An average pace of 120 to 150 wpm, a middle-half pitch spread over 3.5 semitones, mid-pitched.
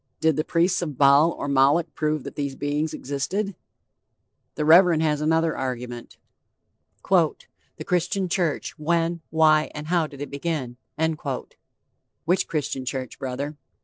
No: slow, 135 wpm; average, 3.1 semitones; medium, 155 Hz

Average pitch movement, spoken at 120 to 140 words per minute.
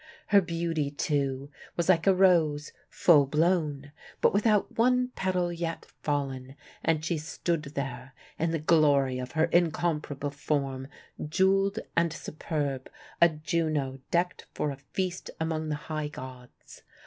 Yes: average, 3.4 semitones; slow, 135 wpm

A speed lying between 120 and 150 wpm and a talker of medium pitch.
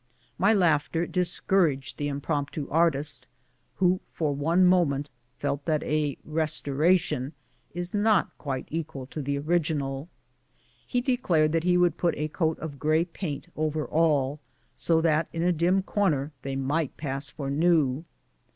No: average, 160 wpm; medium, 155 Hz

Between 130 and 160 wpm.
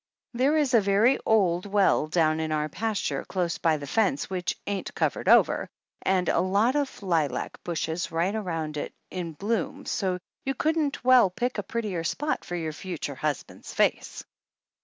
No: average, 175 wpm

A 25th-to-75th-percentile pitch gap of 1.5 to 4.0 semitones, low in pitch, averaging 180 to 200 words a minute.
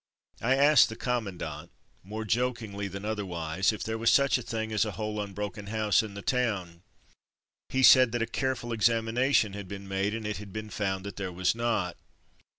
Yes: average, 2.8 semitones; low, 110 Hz; average, 195 wpm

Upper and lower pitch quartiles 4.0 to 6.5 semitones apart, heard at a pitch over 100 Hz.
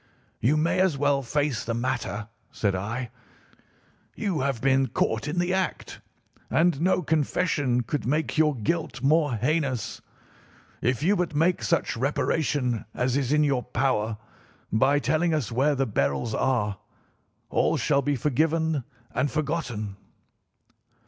Yes: average, 4.4 semitones; medium, 140 Hz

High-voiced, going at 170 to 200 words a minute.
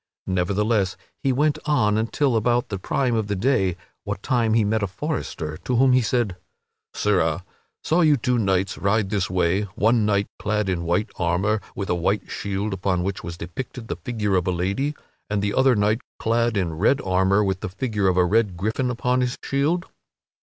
No: low, 105 Hz; average, 195 wpm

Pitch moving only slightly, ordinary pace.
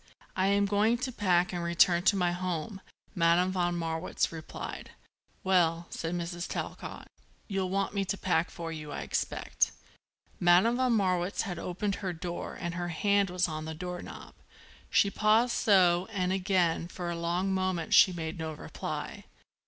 Yes: narrow, 2.3 semitones; average, 170 wpm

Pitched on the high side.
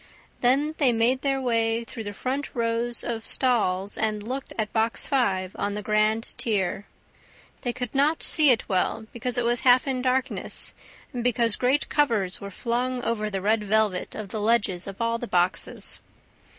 Yes: high, 230 Hz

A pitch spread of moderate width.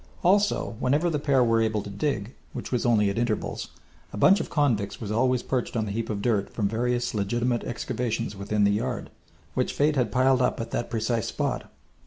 Yes: average, 3.1 semitones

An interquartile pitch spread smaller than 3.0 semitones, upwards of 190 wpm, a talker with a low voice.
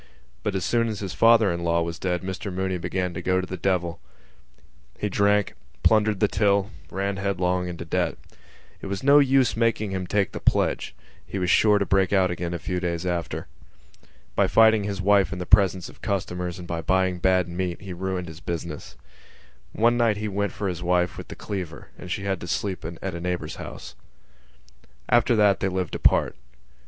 Yes: narrow, 2.4 semitones; average, 200 wpm; very low, 95 Hz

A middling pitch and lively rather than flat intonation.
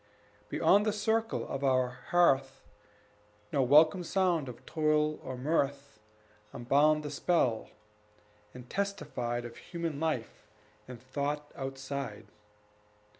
No: medium, 145 Hz; average, 4.0 semitones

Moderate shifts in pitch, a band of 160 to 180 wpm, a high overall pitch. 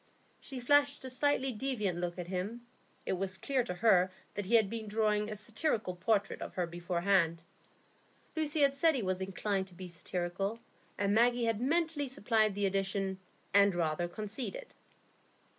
Yes: average, 4.8 semitones; average, 165 wpm; high, 205 Hz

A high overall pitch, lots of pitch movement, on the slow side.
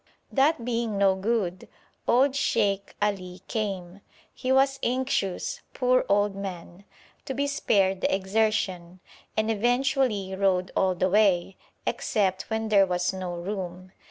No: high, 200 Hz; average, 3.8 semitones; slow, 130 wpm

